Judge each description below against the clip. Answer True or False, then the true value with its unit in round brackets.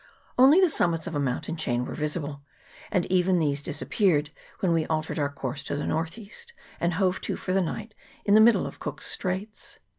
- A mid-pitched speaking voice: True (170 Hz)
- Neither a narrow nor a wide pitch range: True (5.0 semitones)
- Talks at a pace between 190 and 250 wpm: True (205 wpm)